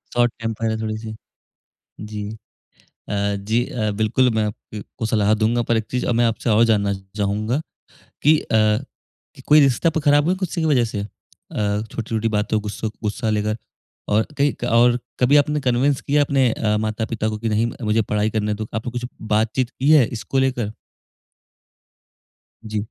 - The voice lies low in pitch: Yes, low, 115 Hz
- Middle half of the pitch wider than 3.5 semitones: No, average, 2.8 semitones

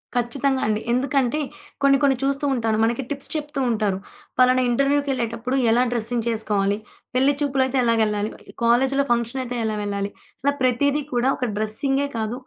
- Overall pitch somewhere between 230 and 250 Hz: Yes, high, 245 Hz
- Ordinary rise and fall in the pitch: Yes, average, 3.4 semitones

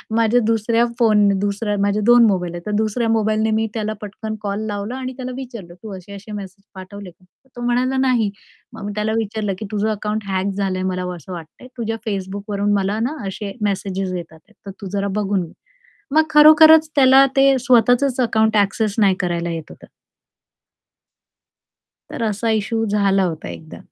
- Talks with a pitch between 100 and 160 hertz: No, high, 210 Hz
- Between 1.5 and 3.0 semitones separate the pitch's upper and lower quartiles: Yes, average, 2.7 semitones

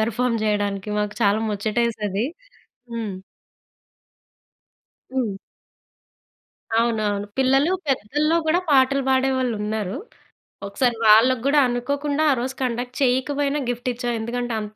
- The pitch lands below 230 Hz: No, high, 240 Hz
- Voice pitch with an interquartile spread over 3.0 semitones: Yes, average, 3.6 semitones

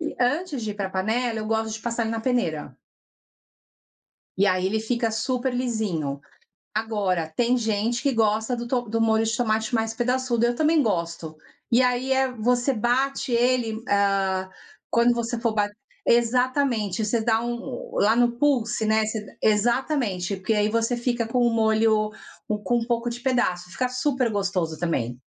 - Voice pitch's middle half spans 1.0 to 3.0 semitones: Yes, average, 2.7 semitones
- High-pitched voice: Yes, high, 225 Hz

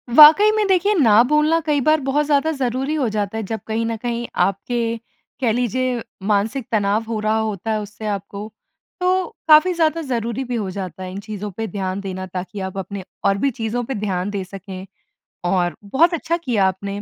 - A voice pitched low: No, high, 225 Hz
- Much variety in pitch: Yes, wide, 5.8 semitones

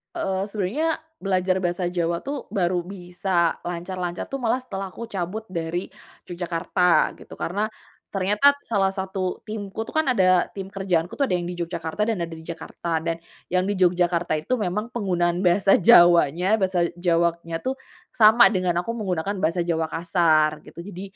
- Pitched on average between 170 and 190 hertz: Yes, medium, 185 Hz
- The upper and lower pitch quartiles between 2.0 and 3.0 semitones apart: Yes, narrow, 2.6 semitones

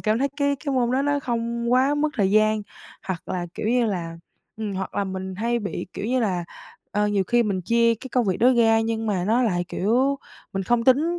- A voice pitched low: No, high, 225 Hz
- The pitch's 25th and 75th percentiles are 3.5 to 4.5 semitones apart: Yes, average, 4.1 semitones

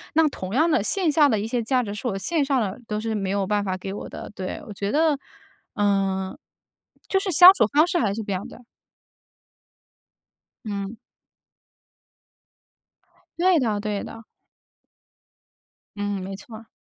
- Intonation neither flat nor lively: No, wide, 6.3 semitones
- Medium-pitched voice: No, high, 215 Hz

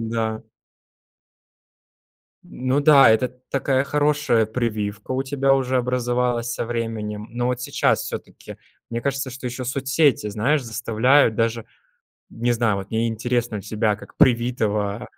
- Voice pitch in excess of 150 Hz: No, low, 120 Hz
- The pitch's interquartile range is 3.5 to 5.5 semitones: No, average, 2.7 semitones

